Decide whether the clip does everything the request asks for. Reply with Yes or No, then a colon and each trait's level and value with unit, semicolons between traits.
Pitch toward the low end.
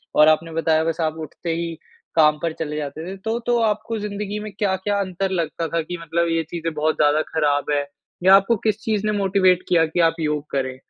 No: medium, 165 Hz